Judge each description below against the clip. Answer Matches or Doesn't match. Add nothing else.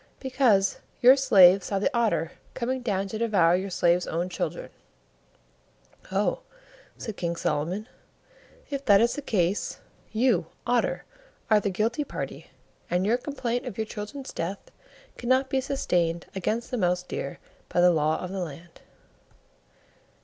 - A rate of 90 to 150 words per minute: Matches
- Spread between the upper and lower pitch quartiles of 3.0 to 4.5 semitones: Doesn't match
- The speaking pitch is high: Matches